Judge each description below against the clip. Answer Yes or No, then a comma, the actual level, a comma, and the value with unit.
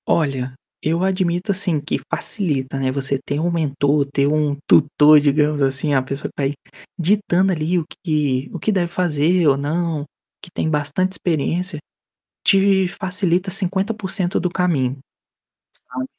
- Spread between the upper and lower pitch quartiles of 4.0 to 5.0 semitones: Yes, average, 4.3 semitones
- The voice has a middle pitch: Yes, medium, 160 Hz